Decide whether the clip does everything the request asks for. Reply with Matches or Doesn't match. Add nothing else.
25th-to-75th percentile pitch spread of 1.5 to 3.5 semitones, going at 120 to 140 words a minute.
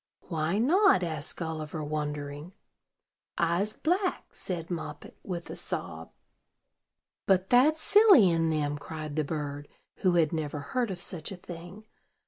Doesn't match